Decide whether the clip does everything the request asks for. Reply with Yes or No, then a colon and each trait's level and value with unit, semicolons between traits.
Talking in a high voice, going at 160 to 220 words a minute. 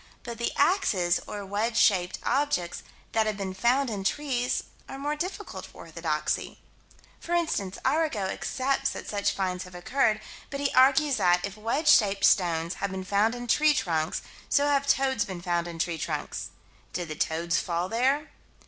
Yes: high, 215 Hz; average, 175 wpm